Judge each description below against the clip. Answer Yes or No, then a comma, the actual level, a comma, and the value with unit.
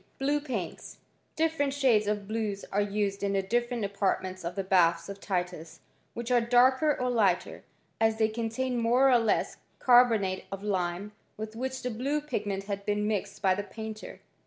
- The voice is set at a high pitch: Yes, high, 215 Hz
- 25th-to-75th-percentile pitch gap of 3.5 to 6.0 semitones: Yes, average, 3.8 semitones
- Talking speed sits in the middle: Yes, average, 175 wpm